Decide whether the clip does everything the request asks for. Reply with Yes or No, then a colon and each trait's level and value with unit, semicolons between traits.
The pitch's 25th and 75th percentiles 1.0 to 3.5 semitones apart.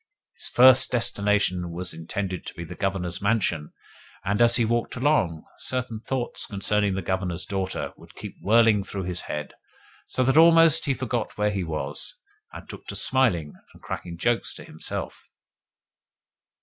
No: average, 5.1 semitones